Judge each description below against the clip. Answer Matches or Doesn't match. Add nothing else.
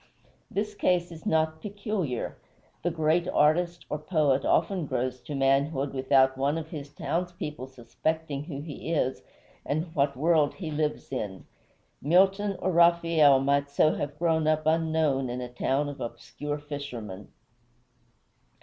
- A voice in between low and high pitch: Matches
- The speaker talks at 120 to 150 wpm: Matches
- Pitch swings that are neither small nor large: Matches